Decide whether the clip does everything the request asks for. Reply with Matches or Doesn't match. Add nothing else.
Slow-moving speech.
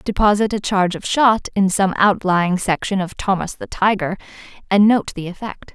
Doesn't match